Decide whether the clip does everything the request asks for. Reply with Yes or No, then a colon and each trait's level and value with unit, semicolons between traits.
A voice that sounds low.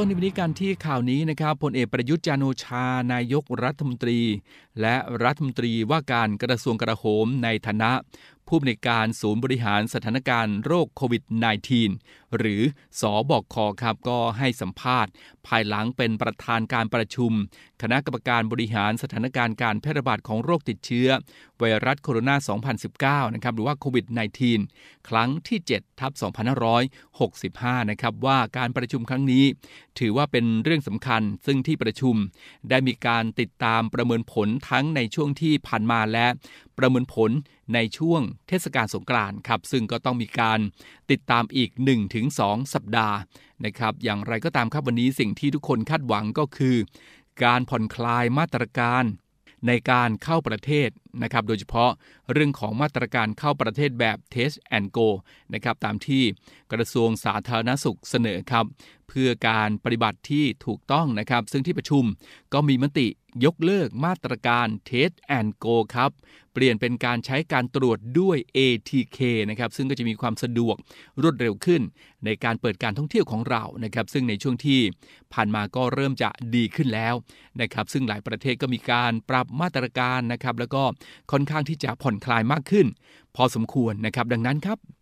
Yes: low, 120 Hz